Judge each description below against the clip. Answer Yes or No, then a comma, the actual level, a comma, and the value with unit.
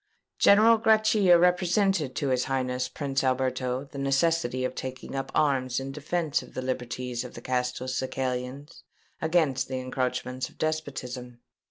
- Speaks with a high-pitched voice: No, low, 130 Hz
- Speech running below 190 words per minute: Yes, average, 140 wpm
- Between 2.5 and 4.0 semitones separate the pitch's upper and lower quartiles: Yes, average, 3.7 semitones